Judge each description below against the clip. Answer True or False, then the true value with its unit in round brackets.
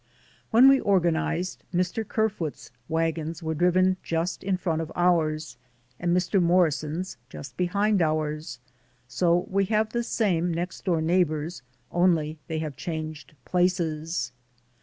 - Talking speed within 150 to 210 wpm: False (135 wpm)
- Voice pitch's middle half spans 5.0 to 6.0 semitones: False (2.8 semitones)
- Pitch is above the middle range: False (170 Hz)